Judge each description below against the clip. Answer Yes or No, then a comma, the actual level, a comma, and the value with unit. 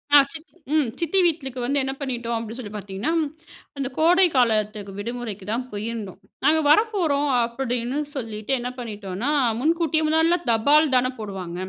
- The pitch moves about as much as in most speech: No, wide, 5.8 semitones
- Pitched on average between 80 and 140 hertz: No, very high, 250 Hz